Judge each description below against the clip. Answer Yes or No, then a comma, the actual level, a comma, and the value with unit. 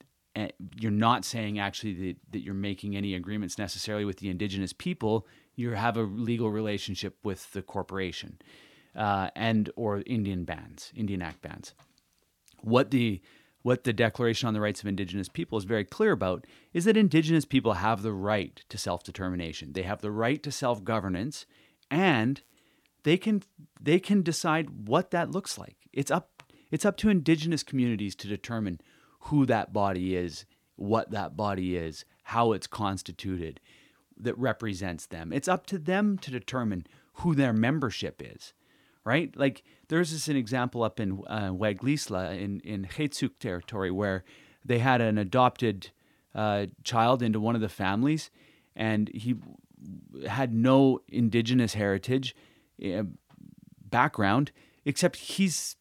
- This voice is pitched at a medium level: No, low, 110 Hz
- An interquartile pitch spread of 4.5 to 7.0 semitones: Yes, average, 5.1 semitones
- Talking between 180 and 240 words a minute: No, average, 155 wpm